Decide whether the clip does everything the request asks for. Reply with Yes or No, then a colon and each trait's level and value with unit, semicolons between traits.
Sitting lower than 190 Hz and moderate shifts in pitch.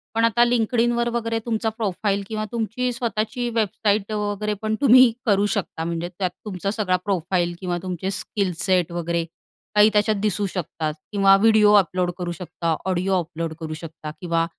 No: high, 200 Hz; average, 3.7 semitones